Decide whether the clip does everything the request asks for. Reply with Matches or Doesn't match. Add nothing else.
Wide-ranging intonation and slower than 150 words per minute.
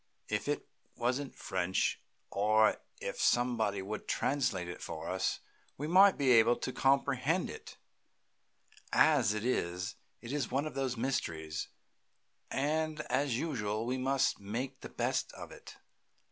Doesn't match